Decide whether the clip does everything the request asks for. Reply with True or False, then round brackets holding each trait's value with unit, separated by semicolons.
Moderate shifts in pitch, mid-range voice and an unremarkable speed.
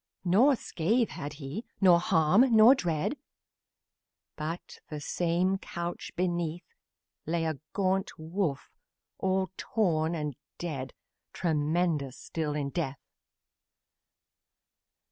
False (3.6 semitones; 170 Hz; 100 wpm)